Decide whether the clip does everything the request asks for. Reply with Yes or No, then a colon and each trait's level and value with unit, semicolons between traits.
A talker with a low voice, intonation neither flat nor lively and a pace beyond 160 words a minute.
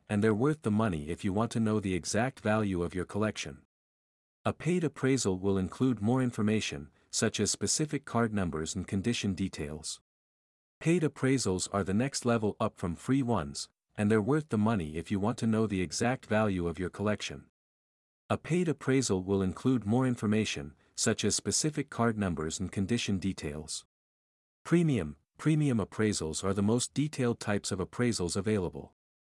Yes: low, 105 Hz; average, 4.9 semitones; average, 170 wpm